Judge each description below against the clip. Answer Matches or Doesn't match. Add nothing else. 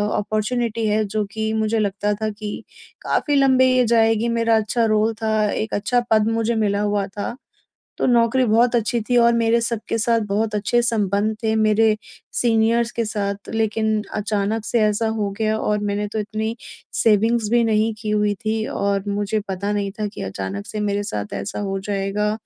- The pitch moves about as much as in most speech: Doesn't match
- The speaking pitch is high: Matches